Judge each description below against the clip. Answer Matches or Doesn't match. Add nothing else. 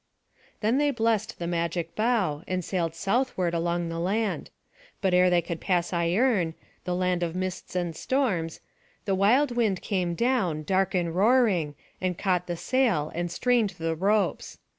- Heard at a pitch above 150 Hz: Matches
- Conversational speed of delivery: Matches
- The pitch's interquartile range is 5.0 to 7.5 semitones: Doesn't match